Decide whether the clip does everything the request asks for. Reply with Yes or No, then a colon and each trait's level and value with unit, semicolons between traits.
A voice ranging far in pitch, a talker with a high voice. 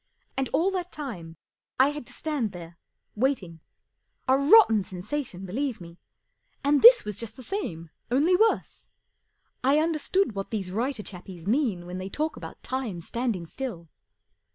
Yes: wide, 8.1 semitones; high, 235 Hz